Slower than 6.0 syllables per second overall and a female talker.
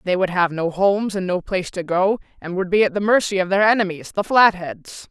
Yes: 5.7 syllables/s; female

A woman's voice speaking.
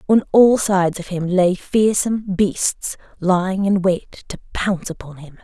Yes: female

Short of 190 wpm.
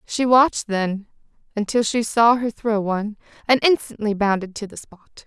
Yes: average, 170 wpm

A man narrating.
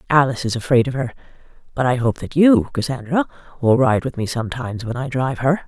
No: female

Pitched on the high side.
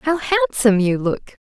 Yes: high, 210 Hz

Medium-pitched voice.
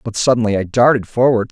No: low, 115 Hz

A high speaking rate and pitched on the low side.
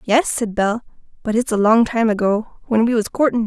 No: fast, 225 wpm; high, 225 Hz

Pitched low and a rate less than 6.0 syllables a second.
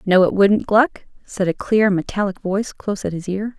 No: high, 200 Hz; 5.1 syllables/s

